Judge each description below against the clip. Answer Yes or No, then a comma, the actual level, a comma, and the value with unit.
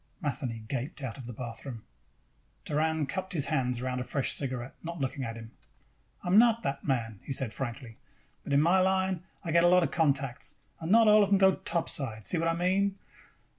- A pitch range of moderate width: No, wide, 6.2 semitones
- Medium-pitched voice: Yes, medium, 145 Hz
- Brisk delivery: Yes, fast, 210 wpm